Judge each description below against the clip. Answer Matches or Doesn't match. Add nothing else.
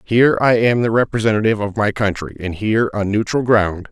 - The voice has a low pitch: Matches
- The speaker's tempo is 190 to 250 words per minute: Matches